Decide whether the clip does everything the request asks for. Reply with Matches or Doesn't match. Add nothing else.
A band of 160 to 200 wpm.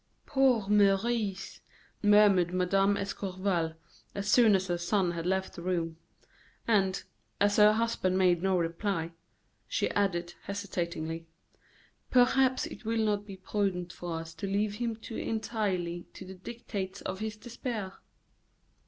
Doesn't match